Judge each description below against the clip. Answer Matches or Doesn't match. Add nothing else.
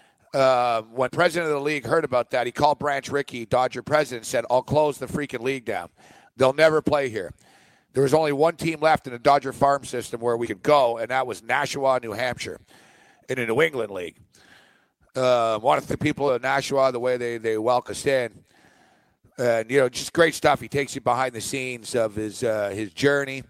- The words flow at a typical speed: Doesn't match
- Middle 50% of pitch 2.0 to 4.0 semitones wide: Matches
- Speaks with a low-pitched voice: Matches